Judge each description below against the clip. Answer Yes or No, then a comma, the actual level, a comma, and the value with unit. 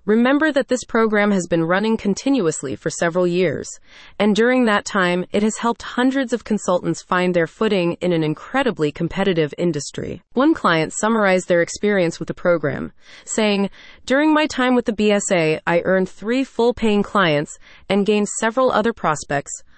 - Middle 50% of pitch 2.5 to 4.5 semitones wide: No, average, 5.1 semitones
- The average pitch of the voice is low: No, high, 200 Hz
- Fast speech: No, average, 165 wpm